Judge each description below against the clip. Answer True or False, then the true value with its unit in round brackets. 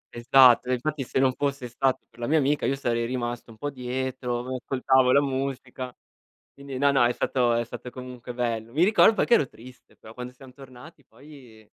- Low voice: True (130 Hz)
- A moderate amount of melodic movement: False (1.9 semitones)